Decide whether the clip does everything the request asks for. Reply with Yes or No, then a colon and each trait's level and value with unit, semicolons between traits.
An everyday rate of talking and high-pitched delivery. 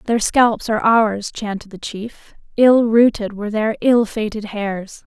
Yes: average, 165 wpm; high, 215 Hz